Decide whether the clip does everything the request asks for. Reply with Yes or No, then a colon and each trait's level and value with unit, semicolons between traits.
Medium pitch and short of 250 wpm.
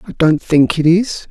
Yes: medium, 165 Hz; fast, 230 wpm